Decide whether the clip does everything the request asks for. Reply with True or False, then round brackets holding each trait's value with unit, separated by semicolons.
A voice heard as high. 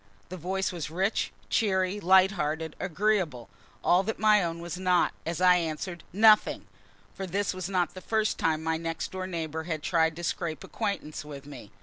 False (180 Hz)